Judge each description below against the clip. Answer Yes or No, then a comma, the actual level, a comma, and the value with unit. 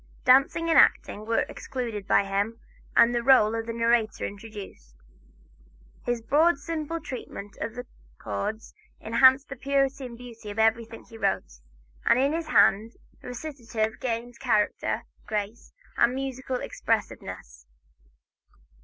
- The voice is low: No, high, 235 Hz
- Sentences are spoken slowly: Yes, slow, 125 wpm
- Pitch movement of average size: Yes, average, 3.4 semitones